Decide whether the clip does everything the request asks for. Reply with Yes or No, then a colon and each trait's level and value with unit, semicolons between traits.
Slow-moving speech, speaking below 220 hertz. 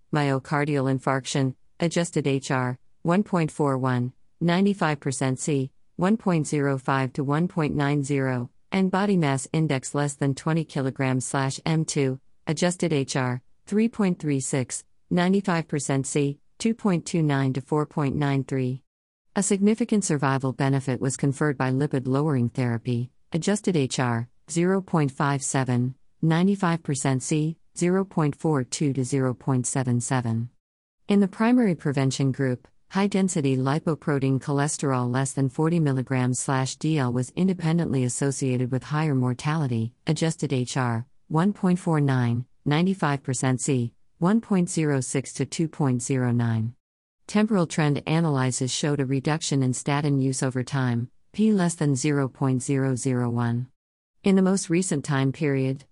Yes: slow, 100 wpm; medium, 140 Hz